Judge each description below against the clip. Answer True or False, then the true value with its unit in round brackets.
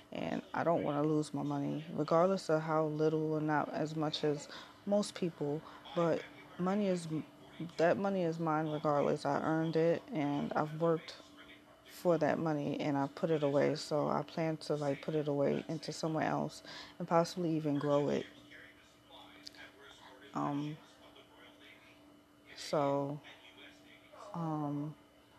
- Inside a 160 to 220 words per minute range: False (140 wpm)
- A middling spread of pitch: False (2.0 semitones)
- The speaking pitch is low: False (155 Hz)